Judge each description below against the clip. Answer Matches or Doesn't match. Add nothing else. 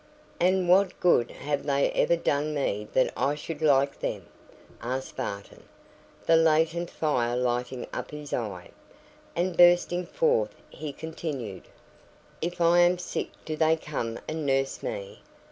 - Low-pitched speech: Doesn't match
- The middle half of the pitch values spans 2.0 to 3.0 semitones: Doesn't match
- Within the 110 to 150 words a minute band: Matches